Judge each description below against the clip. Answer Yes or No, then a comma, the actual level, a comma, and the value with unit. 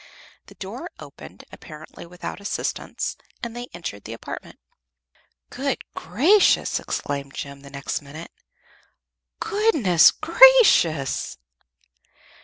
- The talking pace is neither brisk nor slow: No, slow, 95 wpm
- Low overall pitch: No, medium, 170 Hz